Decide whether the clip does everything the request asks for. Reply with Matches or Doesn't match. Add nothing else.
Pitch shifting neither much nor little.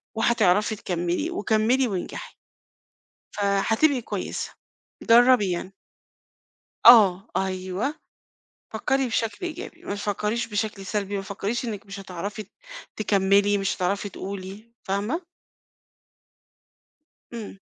Matches